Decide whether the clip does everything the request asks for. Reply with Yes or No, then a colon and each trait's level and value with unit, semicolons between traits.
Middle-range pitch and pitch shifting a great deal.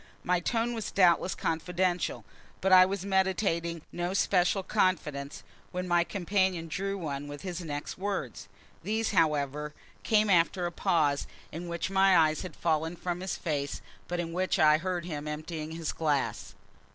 No: medium, 175 Hz; average, 3.2 semitones